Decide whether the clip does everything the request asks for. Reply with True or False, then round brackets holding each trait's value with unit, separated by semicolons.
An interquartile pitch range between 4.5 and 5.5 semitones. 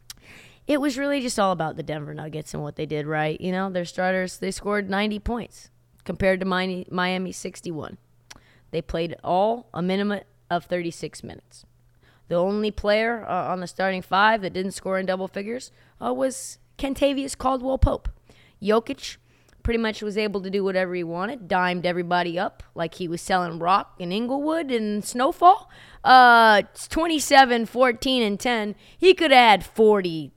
True (5.0 semitones)